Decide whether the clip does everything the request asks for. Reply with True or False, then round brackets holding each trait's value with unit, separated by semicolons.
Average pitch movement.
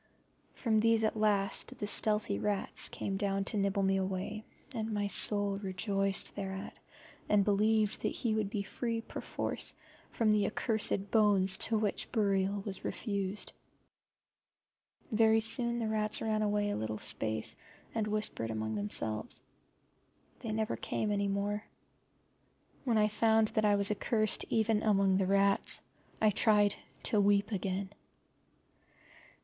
False (1.8 semitones)